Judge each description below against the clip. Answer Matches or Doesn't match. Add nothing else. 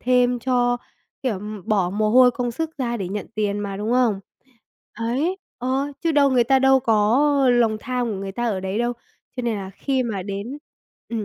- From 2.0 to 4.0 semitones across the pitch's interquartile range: Matches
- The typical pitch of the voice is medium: Doesn't match